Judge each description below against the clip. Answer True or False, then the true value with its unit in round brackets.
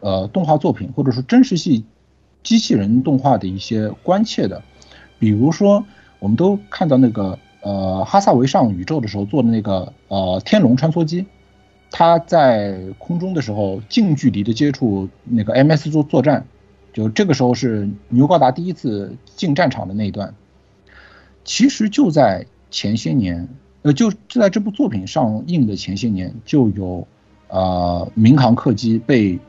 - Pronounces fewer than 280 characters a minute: True (245 characters per minute)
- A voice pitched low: True (125 Hz)